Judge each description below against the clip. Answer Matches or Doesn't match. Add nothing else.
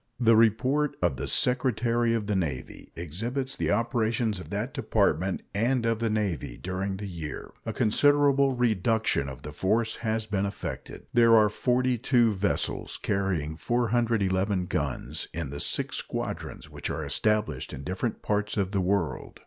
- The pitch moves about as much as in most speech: Matches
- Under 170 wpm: Matches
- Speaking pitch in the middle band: Doesn't match